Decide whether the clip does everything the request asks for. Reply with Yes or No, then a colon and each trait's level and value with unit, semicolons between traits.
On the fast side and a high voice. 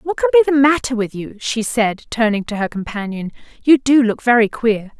Yes: fast, 215 wpm; high, 235 Hz